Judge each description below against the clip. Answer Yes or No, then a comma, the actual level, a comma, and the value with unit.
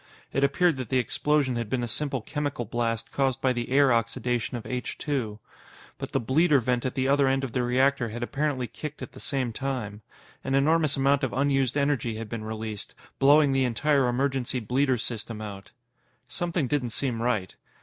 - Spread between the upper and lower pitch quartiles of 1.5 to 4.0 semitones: Yes, average, 2.9 semitones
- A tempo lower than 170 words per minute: No, average, 190 wpm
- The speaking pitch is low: Yes, low, 130 Hz